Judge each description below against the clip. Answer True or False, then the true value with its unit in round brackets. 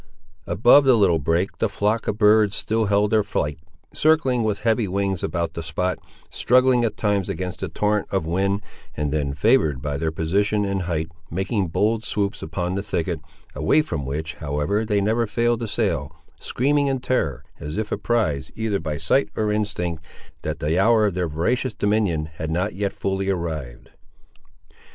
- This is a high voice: False (100 Hz)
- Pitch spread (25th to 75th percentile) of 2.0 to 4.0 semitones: False (5.2 semitones)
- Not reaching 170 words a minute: False (175 wpm)